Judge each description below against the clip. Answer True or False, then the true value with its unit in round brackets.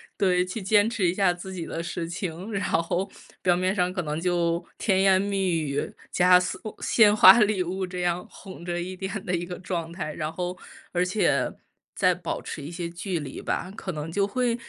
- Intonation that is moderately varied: False (2.0 semitones)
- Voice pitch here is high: False (180 Hz)